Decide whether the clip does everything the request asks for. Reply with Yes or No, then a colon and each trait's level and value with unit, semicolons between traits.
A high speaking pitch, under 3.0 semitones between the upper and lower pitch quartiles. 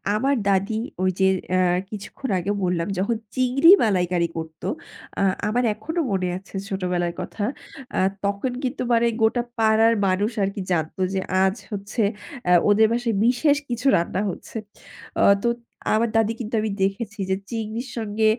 No: high, 210 Hz; average, 3.8 semitones